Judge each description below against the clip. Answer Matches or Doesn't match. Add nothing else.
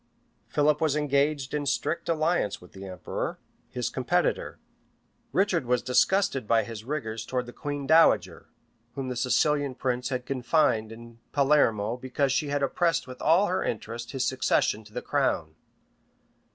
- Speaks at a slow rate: Doesn't match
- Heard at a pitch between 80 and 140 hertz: Matches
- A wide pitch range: Doesn't match